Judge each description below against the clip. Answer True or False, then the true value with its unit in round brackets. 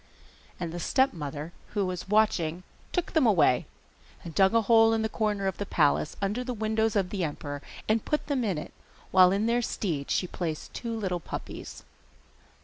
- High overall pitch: True (200 Hz)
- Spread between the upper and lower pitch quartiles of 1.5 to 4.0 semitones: False (4.5 semitones)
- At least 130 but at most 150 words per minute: False (185 wpm)